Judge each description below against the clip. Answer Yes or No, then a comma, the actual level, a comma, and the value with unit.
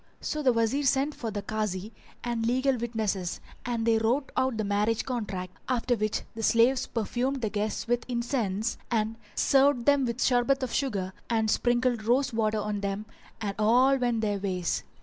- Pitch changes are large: No, average, 3.0 semitones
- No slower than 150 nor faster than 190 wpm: Yes, average, 180 wpm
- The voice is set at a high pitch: Yes, high, 230 Hz